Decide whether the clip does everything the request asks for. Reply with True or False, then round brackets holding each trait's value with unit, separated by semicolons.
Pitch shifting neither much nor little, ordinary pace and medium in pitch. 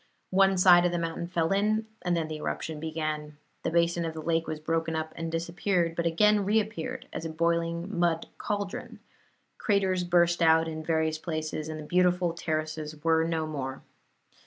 False (2.1 semitones; 180 wpm; 165 Hz)